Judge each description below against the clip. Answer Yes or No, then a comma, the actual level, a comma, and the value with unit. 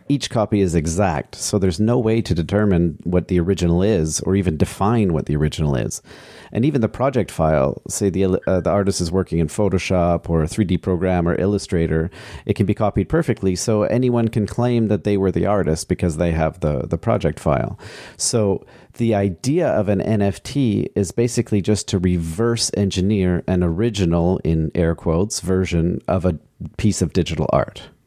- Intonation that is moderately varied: Yes, average, 3.6 semitones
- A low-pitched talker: Yes, very low, 95 Hz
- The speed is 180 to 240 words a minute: Yes, average, 185 wpm